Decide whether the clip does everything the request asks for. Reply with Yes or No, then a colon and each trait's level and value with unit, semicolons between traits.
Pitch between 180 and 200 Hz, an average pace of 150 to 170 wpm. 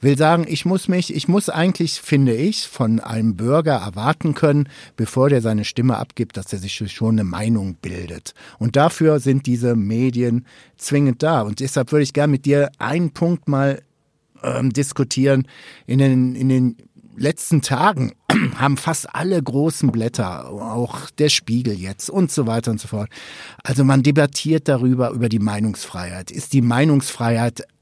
No: low, 135 Hz; average, 165 wpm